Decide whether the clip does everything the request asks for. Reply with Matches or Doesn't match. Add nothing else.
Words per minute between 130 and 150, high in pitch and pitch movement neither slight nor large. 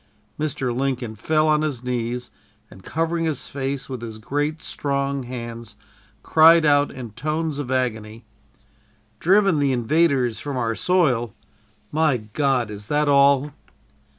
Doesn't match